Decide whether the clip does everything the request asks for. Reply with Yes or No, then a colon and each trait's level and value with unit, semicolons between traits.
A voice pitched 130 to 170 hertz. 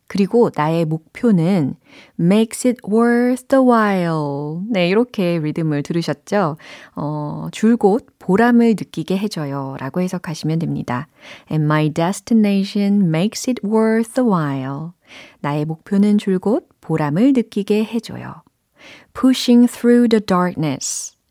No: high, 195 Hz